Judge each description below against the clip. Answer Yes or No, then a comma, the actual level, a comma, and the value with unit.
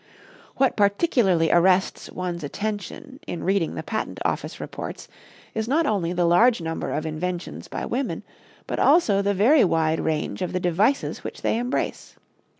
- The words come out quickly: No, average, 155 wpm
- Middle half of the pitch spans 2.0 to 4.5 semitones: No, average, 5.0 semitones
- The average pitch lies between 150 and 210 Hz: Yes, high, 190 Hz